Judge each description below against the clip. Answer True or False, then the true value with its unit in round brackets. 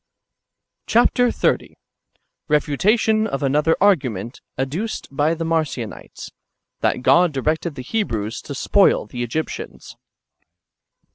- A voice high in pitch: False (155 Hz)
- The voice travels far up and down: True (6.6 semitones)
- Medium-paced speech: False (110 wpm)